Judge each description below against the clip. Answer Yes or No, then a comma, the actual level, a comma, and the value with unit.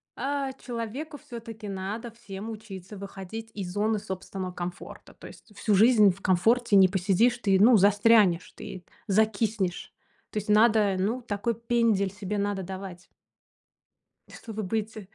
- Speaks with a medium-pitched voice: No, high, 210 Hz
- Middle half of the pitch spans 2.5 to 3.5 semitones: Yes, average, 2.9 semitones